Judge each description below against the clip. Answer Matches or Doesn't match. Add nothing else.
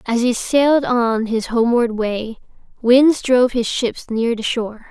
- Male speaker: Doesn't match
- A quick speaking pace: Doesn't match